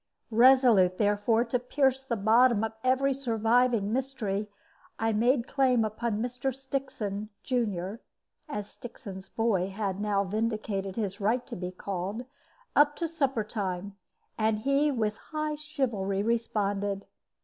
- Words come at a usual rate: No, slow, 130 wpm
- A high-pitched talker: Yes, high, 225 Hz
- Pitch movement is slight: No, average, 4.1 semitones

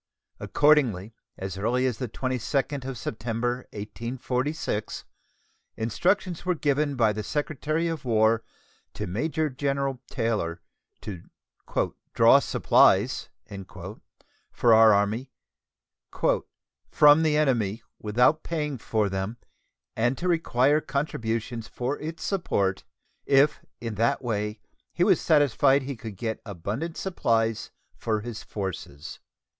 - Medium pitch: No, low, 120 Hz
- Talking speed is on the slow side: Yes, slow, 115 wpm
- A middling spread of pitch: Yes, average, 5.0 semitones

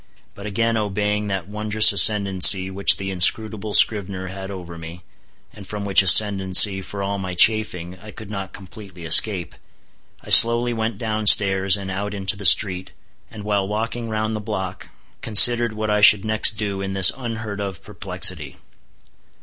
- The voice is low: Yes, low, 100 Hz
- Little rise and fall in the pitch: Yes, narrow, 2.1 semitones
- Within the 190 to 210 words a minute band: No, average, 165 wpm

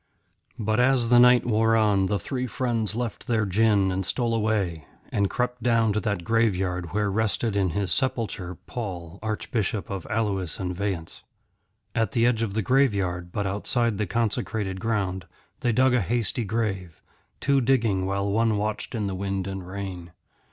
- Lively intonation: No, average, 3.2 semitones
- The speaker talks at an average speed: Yes, average, 170 wpm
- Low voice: Yes, low, 105 Hz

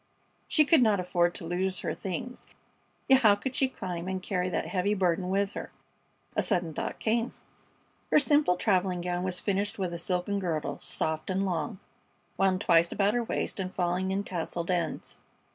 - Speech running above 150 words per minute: Yes, average, 180 wpm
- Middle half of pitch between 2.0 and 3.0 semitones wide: Yes, narrow, 2.4 semitones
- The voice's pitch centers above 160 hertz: Yes, medium, 185 Hz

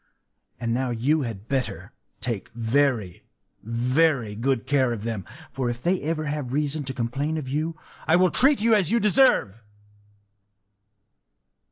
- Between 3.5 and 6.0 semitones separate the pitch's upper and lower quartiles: Yes, average, 5.0 semitones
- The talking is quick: No, average, 150 wpm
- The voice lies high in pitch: No, low, 135 Hz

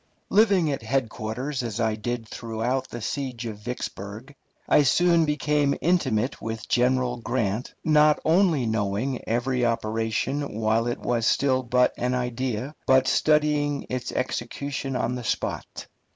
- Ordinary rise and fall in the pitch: Yes, average, 3.8 semitones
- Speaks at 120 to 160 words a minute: Yes, slow, 135 wpm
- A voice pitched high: No, low, 125 Hz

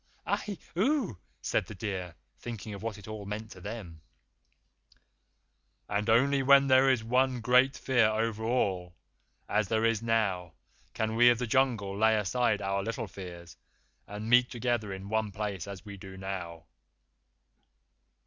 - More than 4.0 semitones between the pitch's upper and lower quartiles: No, average, 3.7 semitones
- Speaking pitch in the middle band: No, low, 110 Hz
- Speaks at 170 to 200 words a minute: No, average, 155 wpm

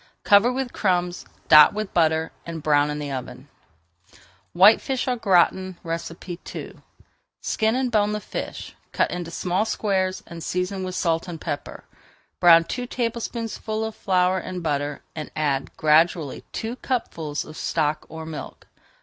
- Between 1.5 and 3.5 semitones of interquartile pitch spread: No, average, 5.0 semitones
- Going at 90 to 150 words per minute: Yes, average, 145 wpm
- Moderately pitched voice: Yes, medium, 180 Hz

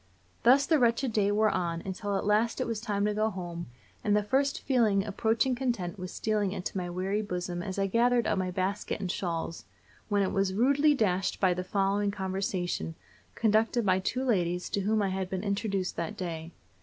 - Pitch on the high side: Yes, high, 200 Hz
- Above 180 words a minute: Yes, average, 200 wpm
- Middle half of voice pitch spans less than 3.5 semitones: Yes, average, 3.1 semitones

